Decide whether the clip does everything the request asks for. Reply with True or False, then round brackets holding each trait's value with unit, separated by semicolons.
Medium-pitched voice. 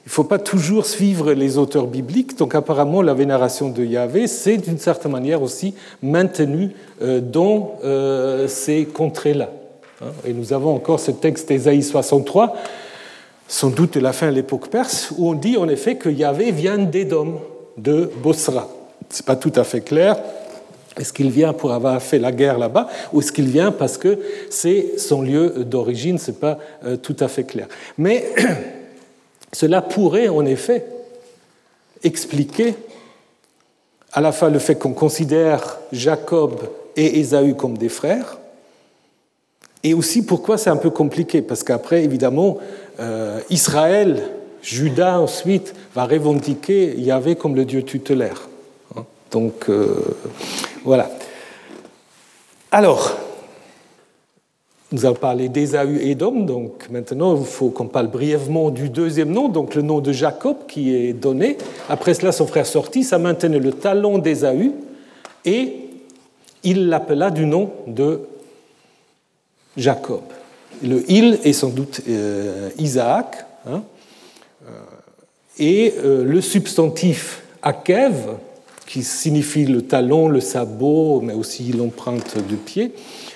True (155 Hz)